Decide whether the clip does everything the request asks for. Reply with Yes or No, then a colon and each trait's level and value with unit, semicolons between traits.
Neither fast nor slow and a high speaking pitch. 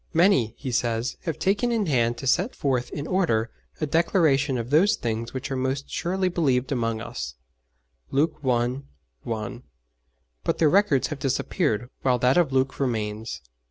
No: average, 160 wpm; low, 135 Hz